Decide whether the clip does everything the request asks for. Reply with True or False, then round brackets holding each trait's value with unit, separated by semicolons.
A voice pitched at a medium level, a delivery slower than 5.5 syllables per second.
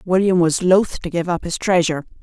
False (175 Hz; 5.6 syllables/s)